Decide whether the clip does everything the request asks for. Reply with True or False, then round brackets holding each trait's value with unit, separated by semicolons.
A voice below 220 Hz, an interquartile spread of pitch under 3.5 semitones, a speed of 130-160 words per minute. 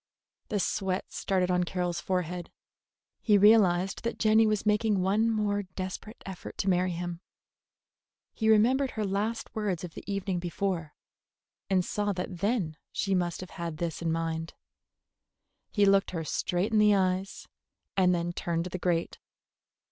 True (190 Hz; 2.9 semitones; 155 wpm)